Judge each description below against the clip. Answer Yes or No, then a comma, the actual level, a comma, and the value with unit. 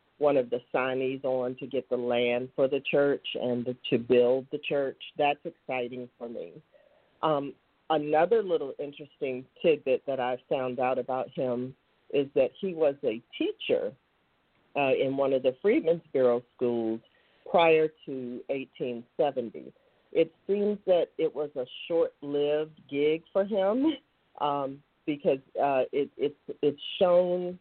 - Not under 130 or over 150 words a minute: Yes, average, 145 wpm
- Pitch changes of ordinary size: No, wide, 7.3 semitones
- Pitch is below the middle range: No, medium, 145 Hz